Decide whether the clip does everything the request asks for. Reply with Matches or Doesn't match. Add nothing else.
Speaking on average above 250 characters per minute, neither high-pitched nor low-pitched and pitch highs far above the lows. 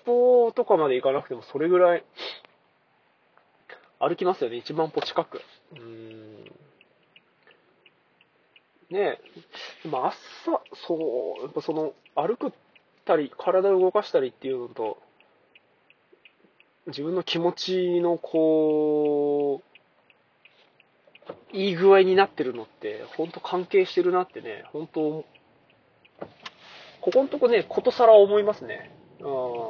Doesn't match